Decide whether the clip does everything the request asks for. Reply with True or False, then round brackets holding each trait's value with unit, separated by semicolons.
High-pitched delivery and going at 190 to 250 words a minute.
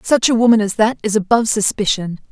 True (220 Hz; 205 wpm)